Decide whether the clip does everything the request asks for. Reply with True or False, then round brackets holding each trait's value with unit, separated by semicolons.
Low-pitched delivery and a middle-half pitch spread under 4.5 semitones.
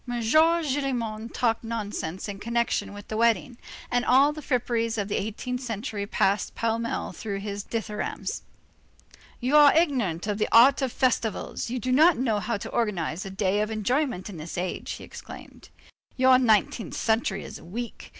False (230 Hz; 3.6 semitones)